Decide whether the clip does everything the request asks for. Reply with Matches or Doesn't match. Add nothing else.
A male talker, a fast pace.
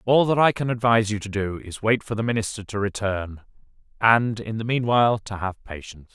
Matches